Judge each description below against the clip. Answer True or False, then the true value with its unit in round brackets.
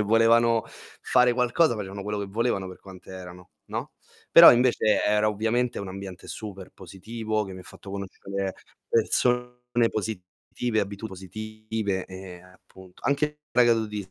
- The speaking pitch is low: True (105 Hz)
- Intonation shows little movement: False (3.5 semitones)